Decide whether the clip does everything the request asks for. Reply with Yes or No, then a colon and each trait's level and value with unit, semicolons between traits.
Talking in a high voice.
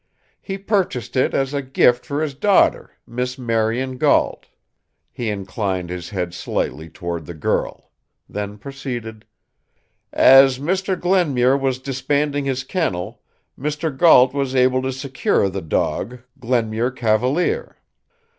No: low, 130 Hz